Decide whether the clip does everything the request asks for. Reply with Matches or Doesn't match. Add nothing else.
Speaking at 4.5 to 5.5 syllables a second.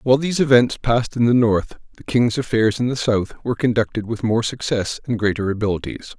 Doesn't match